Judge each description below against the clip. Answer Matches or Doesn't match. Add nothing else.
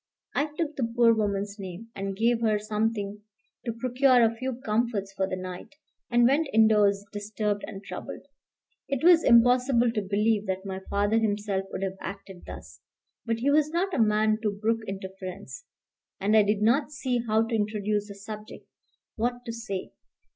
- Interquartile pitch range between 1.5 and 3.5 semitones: Matches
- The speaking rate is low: Doesn't match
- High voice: Matches